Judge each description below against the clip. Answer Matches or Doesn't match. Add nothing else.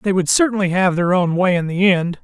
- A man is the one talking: Matches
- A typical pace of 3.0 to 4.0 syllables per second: Doesn't match